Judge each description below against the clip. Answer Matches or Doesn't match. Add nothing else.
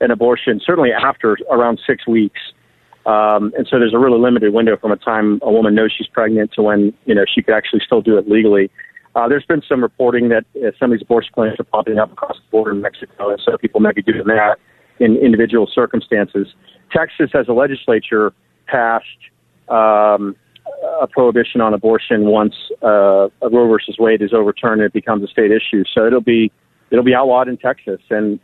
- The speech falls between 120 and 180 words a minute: Doesn't match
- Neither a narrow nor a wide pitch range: Doesn't match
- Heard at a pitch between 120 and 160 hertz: Doesn't match